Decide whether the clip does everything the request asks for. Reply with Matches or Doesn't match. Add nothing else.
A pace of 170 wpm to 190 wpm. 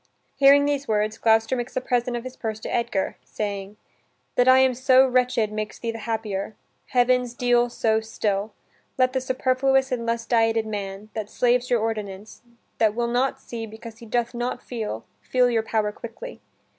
Matches